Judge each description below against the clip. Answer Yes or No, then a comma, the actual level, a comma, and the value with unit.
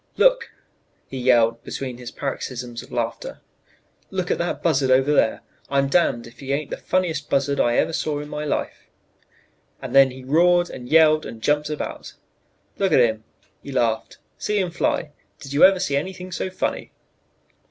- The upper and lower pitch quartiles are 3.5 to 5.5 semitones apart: Yes, average, 5.0 semitones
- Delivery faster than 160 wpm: Yes, average, 175 wpm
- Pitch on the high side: No, medium, 140 Hz